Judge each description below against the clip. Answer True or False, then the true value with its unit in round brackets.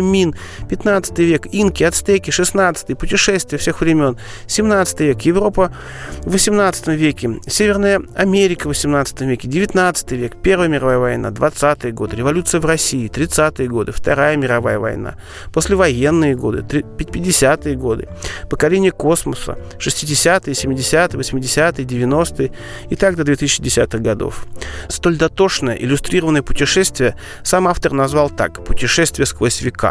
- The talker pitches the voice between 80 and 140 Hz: False (150 Hz)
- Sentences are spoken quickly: False (120 wpm)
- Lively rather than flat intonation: True (5.8 semitones)